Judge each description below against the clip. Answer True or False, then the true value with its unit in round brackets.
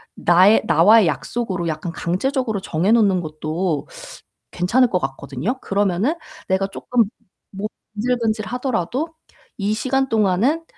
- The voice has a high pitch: True (200 Hz)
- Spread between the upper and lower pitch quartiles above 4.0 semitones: True (5.4 semitones)